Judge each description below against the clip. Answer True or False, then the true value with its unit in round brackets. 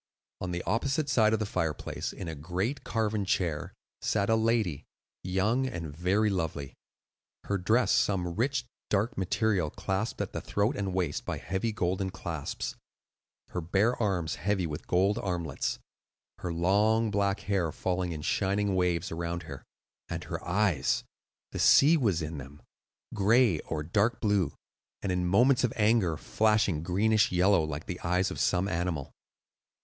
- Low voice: True (95 Hz)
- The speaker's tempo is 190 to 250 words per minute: False (155 wpm)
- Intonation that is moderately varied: True (3.9 semitones)